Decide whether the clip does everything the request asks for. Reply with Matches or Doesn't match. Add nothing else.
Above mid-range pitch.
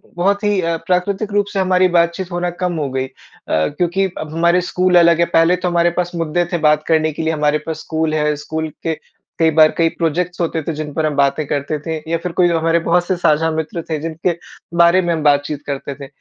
Doesn't match